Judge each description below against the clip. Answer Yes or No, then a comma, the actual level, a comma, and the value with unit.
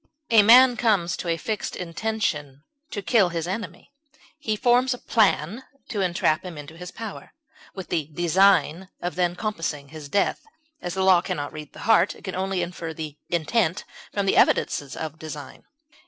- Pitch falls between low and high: Yes, medium, 180 Hz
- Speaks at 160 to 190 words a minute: Yes, average, 180 wpm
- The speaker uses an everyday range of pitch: Yes, average, 4.6 semitones